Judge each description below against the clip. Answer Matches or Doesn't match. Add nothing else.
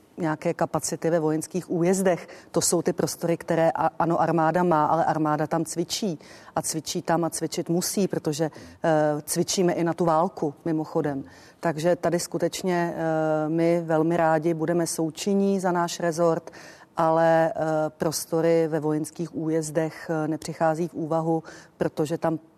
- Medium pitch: Matches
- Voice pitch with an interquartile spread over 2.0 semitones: Doesn't match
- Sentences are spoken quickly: Doesn't match